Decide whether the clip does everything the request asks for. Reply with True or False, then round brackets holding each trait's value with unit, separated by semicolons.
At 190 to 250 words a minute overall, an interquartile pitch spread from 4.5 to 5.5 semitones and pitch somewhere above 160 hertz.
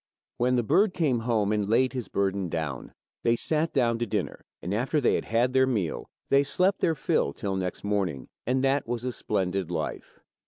False (200 wpm; 5.0 semitones; 115 Hz)